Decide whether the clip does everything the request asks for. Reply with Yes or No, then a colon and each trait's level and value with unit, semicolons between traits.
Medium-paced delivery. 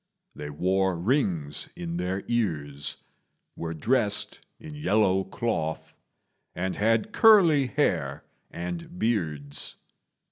No: slow, 100 wpm